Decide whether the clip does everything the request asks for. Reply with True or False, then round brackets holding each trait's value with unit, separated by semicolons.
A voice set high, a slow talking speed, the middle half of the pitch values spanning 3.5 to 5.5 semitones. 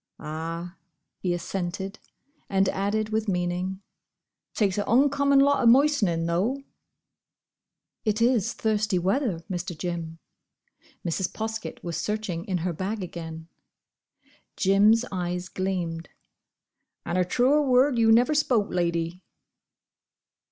True (195 Hz; 115 wpm; 4.3 semitones)